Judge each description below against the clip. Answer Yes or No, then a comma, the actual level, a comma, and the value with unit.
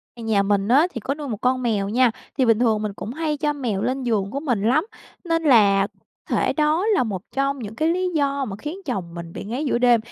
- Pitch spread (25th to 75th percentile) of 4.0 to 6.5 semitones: Yes, wide, 5.5 semitones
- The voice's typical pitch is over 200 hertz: Yes, high, 245 Hz